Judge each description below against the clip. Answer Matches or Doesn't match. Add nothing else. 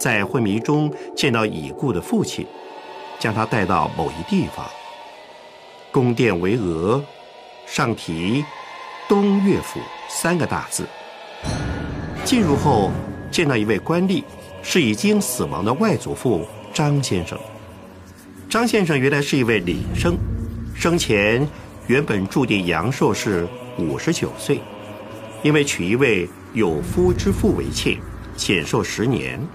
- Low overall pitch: Matches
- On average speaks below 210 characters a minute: Matches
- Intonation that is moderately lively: Doesn't match